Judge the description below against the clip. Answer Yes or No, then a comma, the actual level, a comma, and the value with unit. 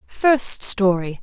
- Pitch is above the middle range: Yes, high, 210 Hz